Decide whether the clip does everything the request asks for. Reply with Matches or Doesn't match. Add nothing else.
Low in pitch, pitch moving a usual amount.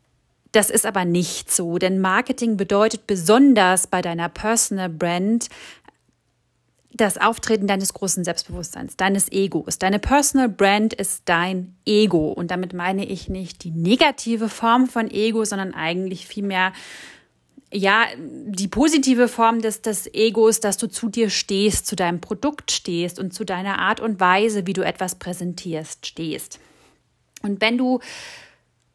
Doesn't match